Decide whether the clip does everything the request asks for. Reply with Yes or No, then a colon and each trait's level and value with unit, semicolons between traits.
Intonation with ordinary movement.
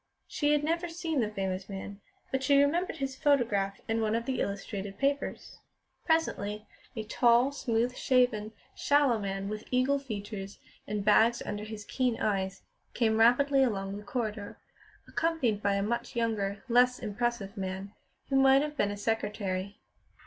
Yes: average, 4.7 semitones